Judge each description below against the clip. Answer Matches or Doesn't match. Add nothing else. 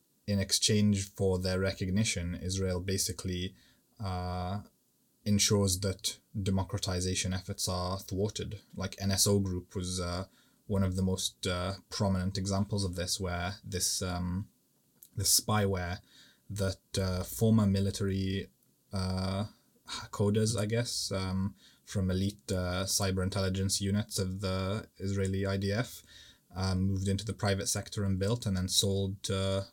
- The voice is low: Matches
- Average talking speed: Doesn't match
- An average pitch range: Doesn't match